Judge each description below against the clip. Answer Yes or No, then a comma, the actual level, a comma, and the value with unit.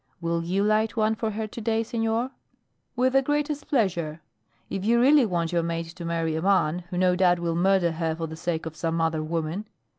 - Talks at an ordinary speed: No, fast, 215 wpm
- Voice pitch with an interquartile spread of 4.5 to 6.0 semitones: Yes, average, 5.0 semitones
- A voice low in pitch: No, medium, 180 Hz